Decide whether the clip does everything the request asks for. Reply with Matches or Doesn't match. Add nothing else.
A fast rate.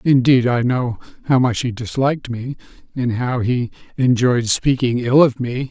Doesn't match